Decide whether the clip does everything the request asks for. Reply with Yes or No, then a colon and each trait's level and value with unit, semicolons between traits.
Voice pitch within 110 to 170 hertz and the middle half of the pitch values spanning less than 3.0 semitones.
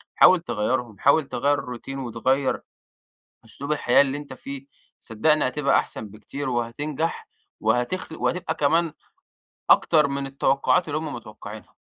No: medium, 140 Hz; average, 3.6 semitones